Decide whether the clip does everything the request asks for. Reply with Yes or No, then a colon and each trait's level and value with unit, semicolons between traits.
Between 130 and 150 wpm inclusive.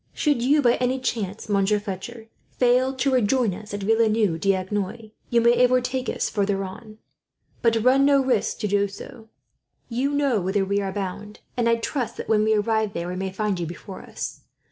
No: average, 190 wpm